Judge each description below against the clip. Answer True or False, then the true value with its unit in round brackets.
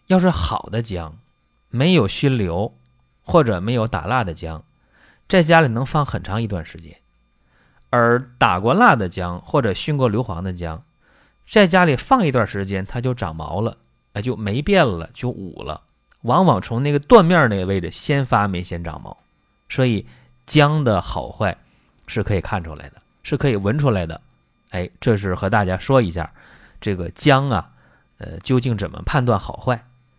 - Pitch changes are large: True (7.0 semitones)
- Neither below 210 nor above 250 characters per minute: True (245 characters per minute)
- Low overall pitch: True (105 Hz)